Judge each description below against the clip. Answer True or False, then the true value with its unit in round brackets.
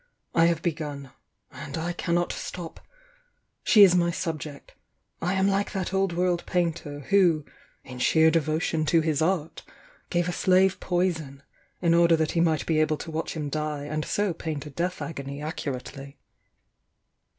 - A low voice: False (165 Hz)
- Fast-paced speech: False (165 wpm)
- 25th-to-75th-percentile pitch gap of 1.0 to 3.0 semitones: True (2.6 semitones)